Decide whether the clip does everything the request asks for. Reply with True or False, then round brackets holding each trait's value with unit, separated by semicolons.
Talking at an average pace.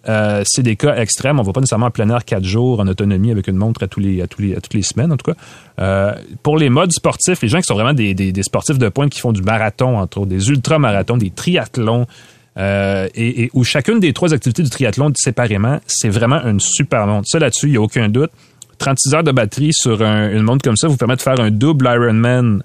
False (260 wpm)